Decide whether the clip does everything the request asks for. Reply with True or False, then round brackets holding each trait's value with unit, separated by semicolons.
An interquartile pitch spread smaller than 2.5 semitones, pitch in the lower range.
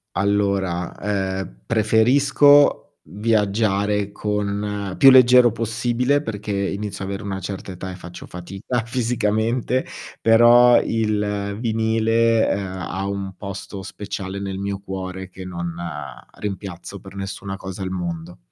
False (2.8 semitones; 100 Hz)